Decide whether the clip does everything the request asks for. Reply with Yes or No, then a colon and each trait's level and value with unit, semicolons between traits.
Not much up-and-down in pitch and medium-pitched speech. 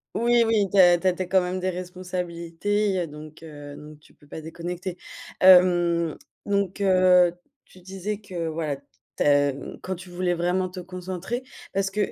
Yes: narrow, 1.9 semitones; medium, 180 Hz